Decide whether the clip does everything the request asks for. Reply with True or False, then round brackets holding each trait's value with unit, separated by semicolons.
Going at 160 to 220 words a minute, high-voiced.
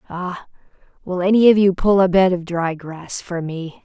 False (205 wpm; 180 Hz)